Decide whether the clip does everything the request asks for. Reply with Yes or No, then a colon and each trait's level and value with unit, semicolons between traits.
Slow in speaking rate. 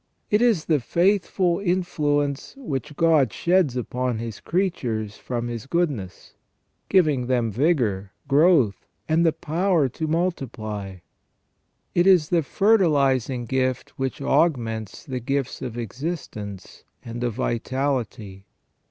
Yes: slow, 115 wpm